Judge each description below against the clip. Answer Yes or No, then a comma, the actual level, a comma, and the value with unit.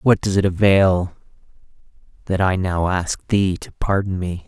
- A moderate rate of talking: Yes, average, 160 wpm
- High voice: No, very low, 95 Hz